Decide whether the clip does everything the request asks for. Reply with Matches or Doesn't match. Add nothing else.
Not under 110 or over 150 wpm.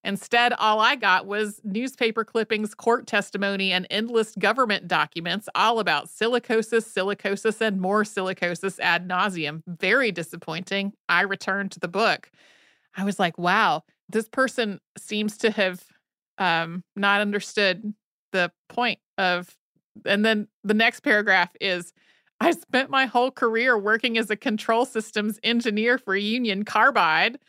Matches